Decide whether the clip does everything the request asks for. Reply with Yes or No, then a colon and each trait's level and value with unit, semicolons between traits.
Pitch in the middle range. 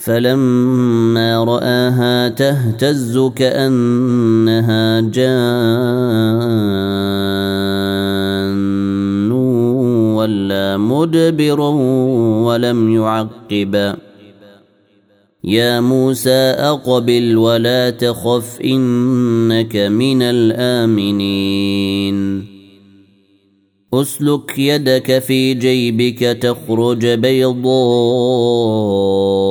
No: low, 115 Hz